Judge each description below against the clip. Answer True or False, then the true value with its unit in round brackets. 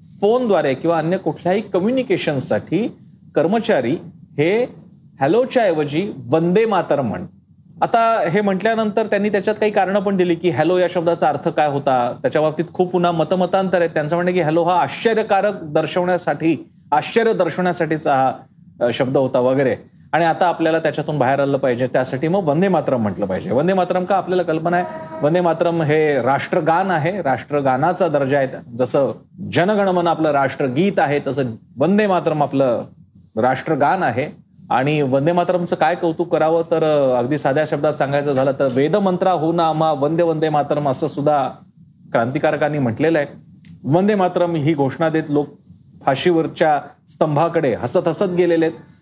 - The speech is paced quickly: True (150 wpm)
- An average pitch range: True (3.5 semitones)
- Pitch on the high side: False (165 Hz)